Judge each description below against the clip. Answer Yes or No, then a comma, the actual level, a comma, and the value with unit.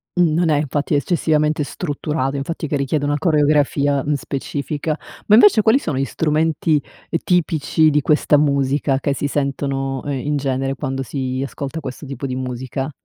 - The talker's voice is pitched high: No, medium, 145 Hz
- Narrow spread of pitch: Yes, narrow, 2.2 semitones